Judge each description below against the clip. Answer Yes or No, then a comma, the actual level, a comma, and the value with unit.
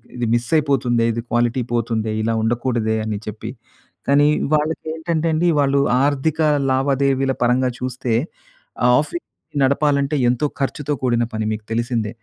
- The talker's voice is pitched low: Yes, low, 130 Hz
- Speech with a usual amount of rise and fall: Yes, average, 3.3 semitones